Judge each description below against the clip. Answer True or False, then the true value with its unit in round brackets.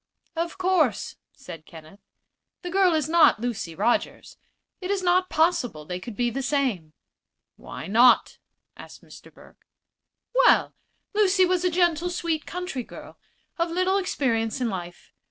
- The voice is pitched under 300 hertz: False (315 Hz)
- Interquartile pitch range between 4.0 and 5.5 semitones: False (8.2 semitones)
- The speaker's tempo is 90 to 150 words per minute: True (145 wpm)